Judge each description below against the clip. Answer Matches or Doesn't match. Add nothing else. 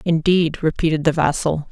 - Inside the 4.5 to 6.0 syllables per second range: Matches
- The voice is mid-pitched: Matches